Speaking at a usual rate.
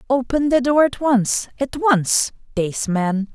Yes: average, 160 wpm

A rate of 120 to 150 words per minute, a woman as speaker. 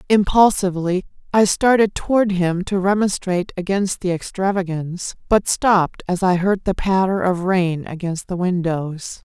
Yes: average, 140 wpm; female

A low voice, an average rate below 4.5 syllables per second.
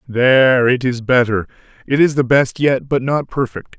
No: low, 130 Hz; 4.6 syllables/s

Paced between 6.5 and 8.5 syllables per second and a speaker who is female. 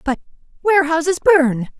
No: 5.3 syllables/s; female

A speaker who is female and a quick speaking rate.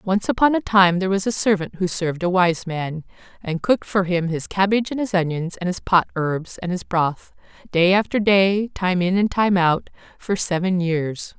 Yes: female; fast, 210 wpm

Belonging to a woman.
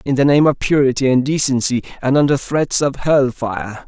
No: male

